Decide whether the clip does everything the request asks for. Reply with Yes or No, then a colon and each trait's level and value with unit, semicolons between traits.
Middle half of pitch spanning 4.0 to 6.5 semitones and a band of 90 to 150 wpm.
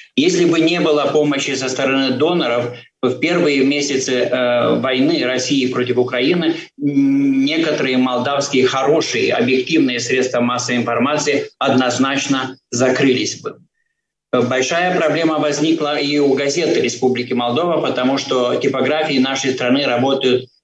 No: average, 3.1 semitones; average, 115 wpm